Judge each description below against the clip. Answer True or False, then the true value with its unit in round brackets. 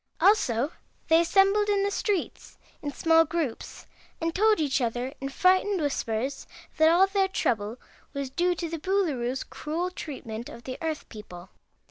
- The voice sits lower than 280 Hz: False (320 Hz)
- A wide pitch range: True (6.3 semitones)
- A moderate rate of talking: True (155 wpm)